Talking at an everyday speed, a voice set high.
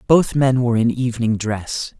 No: average, 180 wpm; low, 120 Hz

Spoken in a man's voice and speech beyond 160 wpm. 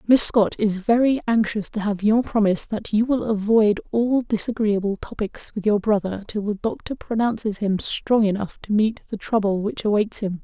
No: female; average, 190 wpm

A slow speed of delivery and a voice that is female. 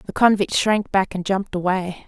No: fast, 205 wpm; female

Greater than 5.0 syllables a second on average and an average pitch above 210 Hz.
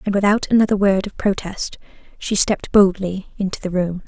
No: 5.5 syllables/s; high, 195 Hz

